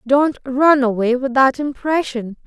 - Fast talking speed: No, average, 145 wpm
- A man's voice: No, female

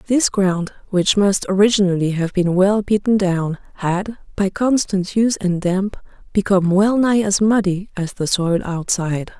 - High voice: Yes, high, 195 Hz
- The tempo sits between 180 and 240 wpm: No, average, 160 wpm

